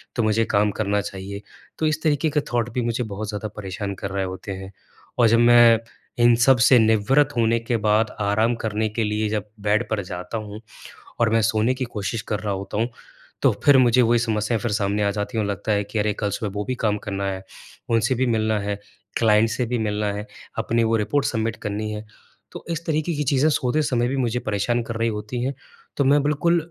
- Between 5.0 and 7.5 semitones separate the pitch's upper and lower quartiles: No, average, 2.7 semitones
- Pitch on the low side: Yes, low, 110 Hz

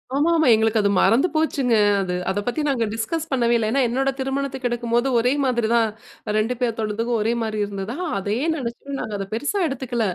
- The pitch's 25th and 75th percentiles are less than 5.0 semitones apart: Yes, average, 3.3 semitones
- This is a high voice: Yes, high, 235 Hz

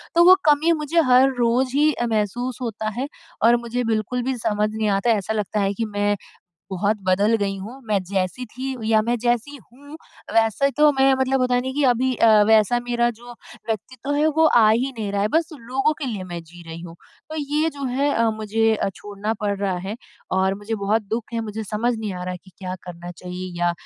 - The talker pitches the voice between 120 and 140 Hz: No, high, 225 Hz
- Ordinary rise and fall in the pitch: Yes, average, 4.0 semitones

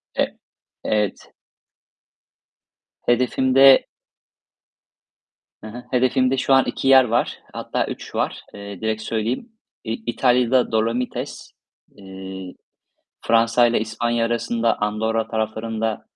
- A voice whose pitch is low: Yes, low, 115 Hz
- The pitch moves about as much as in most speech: No, narrow, 2.3 semitones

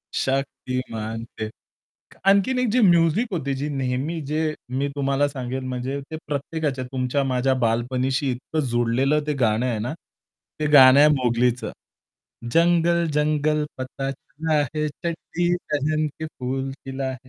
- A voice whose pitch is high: No, low, 135 Hz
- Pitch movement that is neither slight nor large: Yes, average, 3.2 semitones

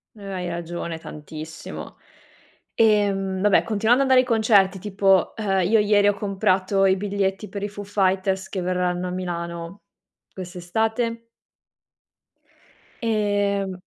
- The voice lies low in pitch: No, high, 195 Hz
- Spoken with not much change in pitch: Yes, narrow, 2.2 semitones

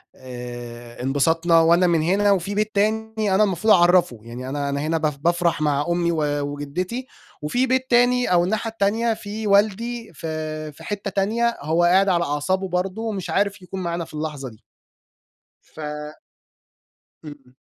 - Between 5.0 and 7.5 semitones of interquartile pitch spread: Yes, wide, 5.5 semitones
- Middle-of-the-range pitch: Yes, medium, 175 Hz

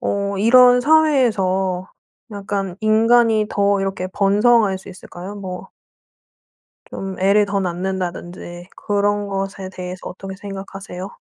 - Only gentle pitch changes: Yes, narrow, 1.7 semitones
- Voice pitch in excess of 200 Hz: No, high, 195 Hz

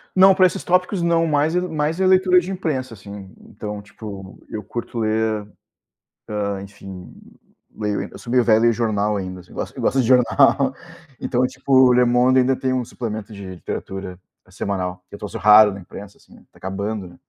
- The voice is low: Yes, low, 110 Hz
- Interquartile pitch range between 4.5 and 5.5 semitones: Yes, average, 5.0 semitones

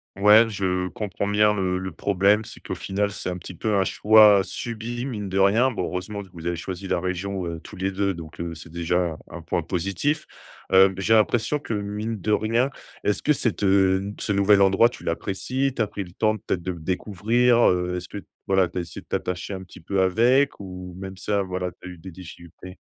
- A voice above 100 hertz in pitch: No, very low, 95 Hz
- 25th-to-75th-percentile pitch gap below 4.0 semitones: Yes, average, 2.7 semitones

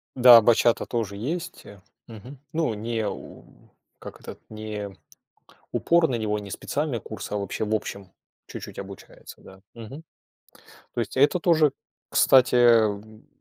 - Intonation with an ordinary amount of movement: Yes, average, 3.9 semitones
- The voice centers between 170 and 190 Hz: No, low, 115 Hz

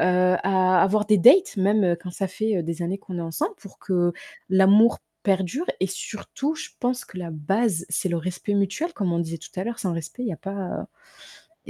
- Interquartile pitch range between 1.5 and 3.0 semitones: No, average, 3.4 semitones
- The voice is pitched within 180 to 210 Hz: Yes, high, 190 Hz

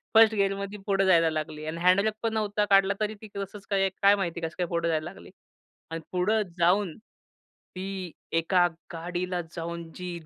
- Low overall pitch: No, medium, 185 Hz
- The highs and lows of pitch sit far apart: No, average, 2.8 semitones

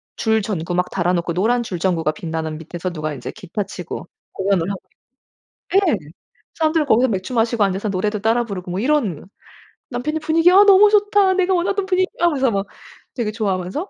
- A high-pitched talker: Yes, high, 215 Hz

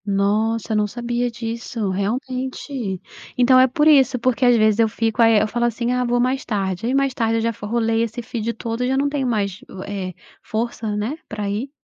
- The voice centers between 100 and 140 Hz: No, high, 230 Hz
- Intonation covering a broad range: No, average, 2.7 semitones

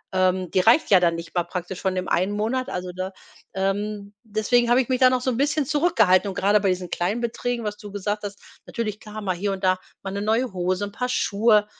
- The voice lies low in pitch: No, high, 205 Hz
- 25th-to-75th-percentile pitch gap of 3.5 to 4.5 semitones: Yes, average, 3.8 semitones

